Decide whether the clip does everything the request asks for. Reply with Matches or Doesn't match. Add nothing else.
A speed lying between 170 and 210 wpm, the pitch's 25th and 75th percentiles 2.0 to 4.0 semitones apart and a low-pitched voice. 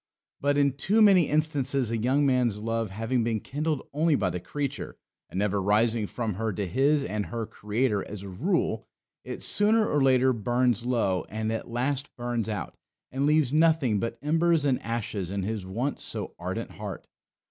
Doesn't match